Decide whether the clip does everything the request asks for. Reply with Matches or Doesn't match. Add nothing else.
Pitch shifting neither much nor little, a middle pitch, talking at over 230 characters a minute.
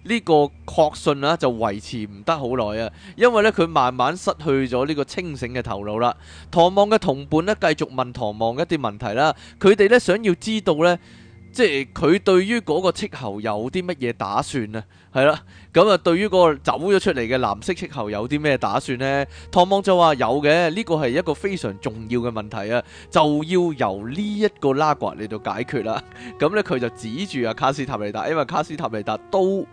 Doesn't match